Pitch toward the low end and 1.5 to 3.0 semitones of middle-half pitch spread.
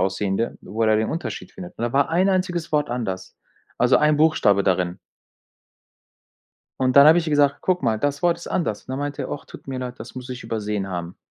No: low, 125 Hz; wide, 6.3 semitones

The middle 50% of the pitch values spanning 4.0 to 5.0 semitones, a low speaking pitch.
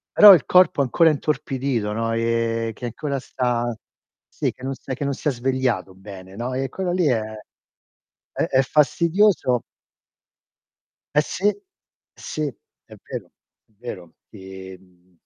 Yes: average, 4.6 semitones; low, 125 Hz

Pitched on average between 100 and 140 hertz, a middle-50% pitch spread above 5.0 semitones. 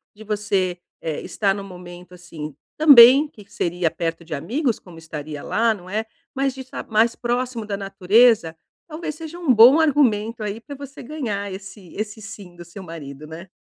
No: high, 210 Hz; wide, 5.6 semitones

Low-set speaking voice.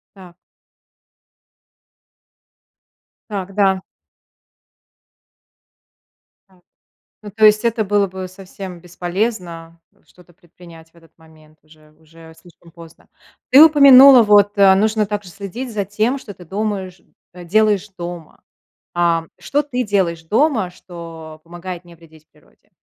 No: medium, 185 Hz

